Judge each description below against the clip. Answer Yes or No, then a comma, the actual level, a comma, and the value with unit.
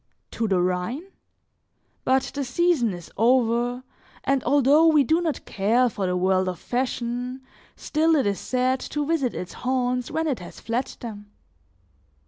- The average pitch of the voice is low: No, very high, 250 Hz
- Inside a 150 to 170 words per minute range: Yes, average, 155 wpm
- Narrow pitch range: No, average, 4.4 semitones